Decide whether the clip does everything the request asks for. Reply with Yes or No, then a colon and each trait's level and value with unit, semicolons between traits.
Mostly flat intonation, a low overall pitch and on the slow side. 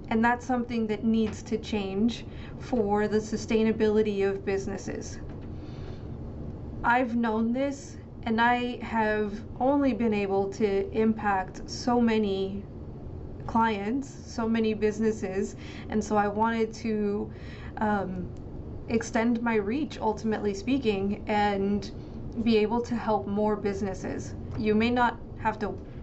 No: narrow, 2.0 semitones; high, 220 Hz; slow, 120 wpm